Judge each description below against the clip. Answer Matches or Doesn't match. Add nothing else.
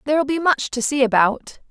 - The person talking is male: Doesn't match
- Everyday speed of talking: Doesn't match